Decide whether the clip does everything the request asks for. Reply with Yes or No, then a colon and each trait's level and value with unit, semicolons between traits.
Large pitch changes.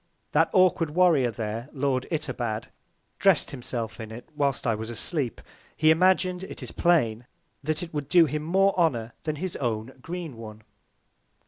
Yes: wide, 6.4 semitones